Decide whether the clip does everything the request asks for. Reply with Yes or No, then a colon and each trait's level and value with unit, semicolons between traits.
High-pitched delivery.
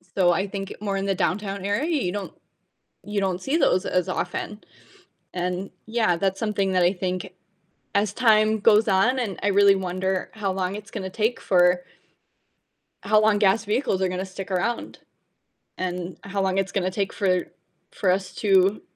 Yes: high, 195 Hz